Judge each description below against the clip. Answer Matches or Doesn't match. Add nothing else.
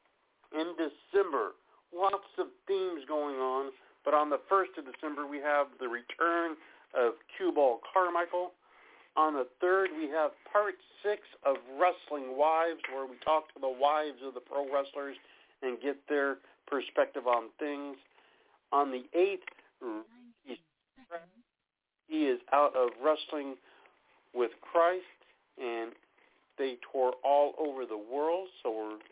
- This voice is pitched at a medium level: Matches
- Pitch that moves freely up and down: Doesn't match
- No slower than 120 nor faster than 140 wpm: Matches